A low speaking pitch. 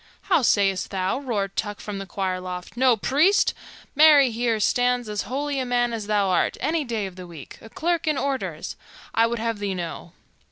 No: high, 225 Hz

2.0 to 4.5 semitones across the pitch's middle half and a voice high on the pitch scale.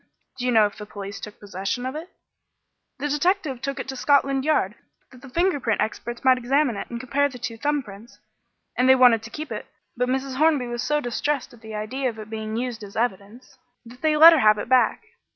Yes: average, 4.1 semitones; very high, 250 Hz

